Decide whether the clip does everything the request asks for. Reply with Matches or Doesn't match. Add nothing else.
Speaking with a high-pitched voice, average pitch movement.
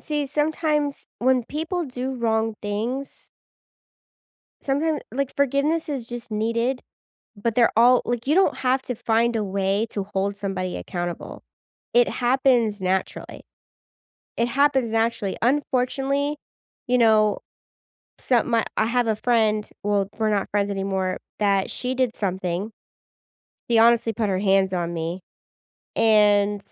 Matches